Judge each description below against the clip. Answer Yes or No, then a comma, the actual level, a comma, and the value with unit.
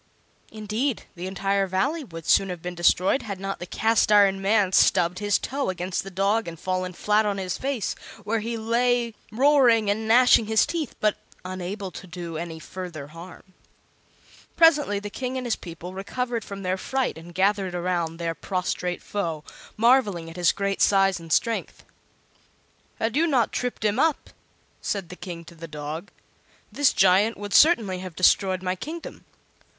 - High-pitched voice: Yes, high, 195 Hz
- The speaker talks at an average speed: Yes, average, 170 wpm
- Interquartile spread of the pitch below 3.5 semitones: No, average, 4.1 semitones